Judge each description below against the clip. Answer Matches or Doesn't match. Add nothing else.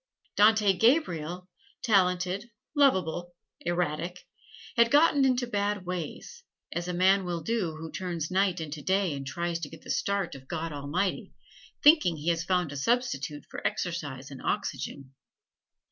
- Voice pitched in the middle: Matches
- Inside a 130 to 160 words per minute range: Matches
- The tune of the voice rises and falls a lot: Doesn't match